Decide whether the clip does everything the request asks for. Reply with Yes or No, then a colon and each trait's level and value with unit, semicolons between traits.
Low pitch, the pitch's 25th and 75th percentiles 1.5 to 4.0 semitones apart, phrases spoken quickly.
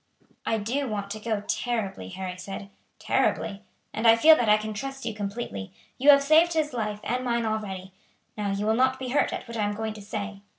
No: high, 220 Hz; average, 3.4 semitones; fast, 220 wpm